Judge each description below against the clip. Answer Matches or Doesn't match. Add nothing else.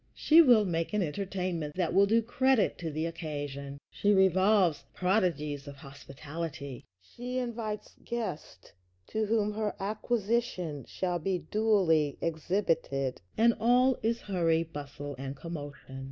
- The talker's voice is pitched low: Doesn't match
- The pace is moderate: Doesn't match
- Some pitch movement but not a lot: Doesn't match